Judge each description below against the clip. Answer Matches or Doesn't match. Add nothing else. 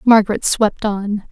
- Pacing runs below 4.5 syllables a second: Matches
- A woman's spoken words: Matches